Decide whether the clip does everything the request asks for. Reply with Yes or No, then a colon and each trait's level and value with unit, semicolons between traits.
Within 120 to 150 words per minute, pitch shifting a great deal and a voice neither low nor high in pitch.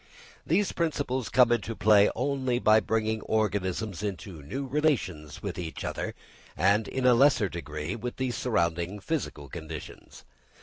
No: average, 140 wpm; wide, 6.5 semitones; low, 110 Hz